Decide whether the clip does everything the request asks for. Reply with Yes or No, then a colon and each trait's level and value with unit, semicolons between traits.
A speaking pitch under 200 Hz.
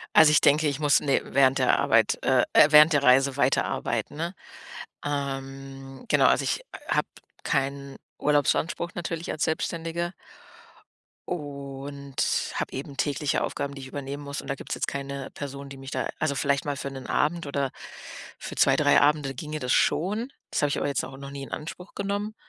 Yes: medium, 140 Hz